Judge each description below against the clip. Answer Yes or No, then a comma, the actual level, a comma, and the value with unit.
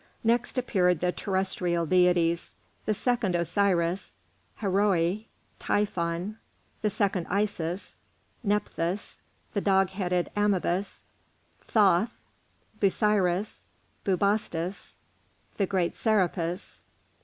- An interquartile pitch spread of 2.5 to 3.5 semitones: Yes, average, 2.8 semitones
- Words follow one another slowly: Yes, slow, 85 wpm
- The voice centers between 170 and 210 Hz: Yes, high, 190 Hz